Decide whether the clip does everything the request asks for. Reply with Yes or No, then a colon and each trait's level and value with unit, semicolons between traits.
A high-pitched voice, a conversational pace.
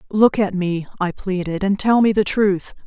No: high, 195 Hz; fast, 210 wpm